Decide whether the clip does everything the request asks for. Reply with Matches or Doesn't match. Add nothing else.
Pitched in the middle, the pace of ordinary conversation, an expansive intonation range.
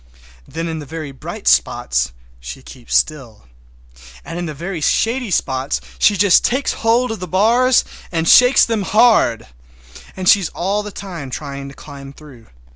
Matches